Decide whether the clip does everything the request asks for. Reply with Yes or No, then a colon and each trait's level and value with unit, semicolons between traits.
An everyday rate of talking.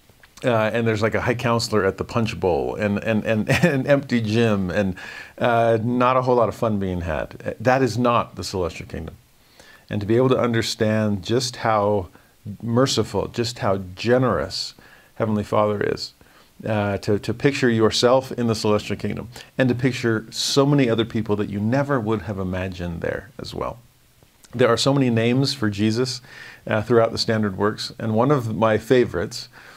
Yes: average, 180 wpm